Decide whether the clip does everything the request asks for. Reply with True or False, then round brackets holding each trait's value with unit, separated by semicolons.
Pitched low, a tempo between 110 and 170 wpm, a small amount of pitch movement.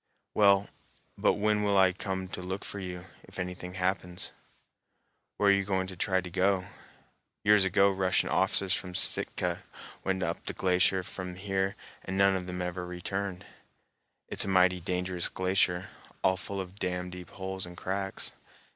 True (95 Hz; 160 wpm; 1.3 semitones)